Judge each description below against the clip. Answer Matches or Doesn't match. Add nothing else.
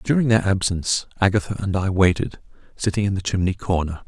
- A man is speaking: Matches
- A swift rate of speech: Doesn't match